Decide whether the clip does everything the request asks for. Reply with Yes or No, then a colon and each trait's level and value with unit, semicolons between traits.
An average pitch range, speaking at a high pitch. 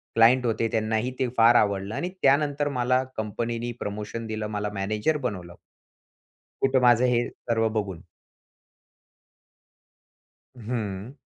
No: average, 3.0 semitones; low, 115 Hz